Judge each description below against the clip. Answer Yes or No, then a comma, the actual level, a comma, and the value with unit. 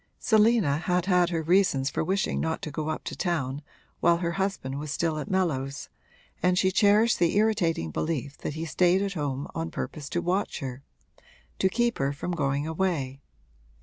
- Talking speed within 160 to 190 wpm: Yes, average, 180 wpm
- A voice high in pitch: No, medium, 170 Hz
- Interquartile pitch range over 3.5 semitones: Yes, average, 4.8 semitones